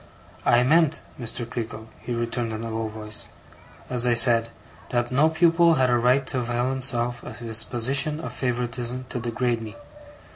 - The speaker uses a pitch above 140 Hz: No, low, 120 Hz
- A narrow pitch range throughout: Yes, narrow, 1.9 semitones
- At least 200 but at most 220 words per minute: No, average, 175 wpm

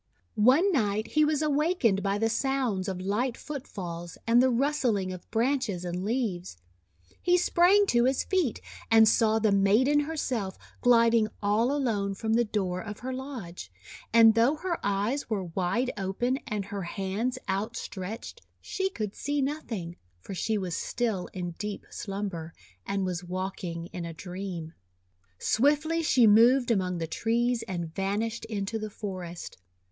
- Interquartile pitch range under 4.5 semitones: No, average, 5.1 semitones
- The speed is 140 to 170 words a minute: Yes, average, 155 wpm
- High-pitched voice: Yes, high, 220 Hz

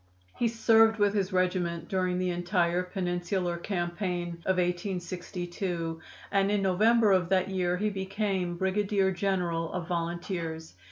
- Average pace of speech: No, slow, 130 wpm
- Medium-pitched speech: Yes, medium, 180 Hz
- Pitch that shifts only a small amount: Yes, narrow, 2.1 semitones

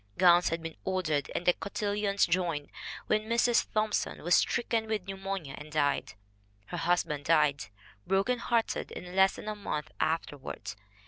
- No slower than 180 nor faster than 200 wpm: No, average, 170 wpm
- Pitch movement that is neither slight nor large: Yes, average, 4.9 semitones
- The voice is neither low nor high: Yes, medium, 180 Hz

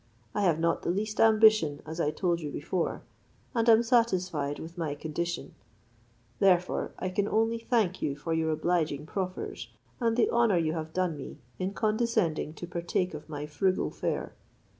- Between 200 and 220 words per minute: No, average, 170 wpm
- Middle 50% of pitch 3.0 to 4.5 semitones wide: No, average, 5.2 semitones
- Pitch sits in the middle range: Yes, medium, 175 Hz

